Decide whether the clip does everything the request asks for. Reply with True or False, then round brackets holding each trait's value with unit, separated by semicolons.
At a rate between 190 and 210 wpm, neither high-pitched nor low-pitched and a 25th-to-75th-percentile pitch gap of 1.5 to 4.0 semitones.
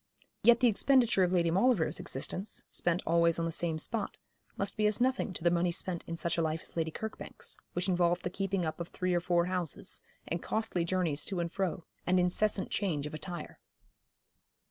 True (200 wpm; 175 Hz; 2.7 semitones)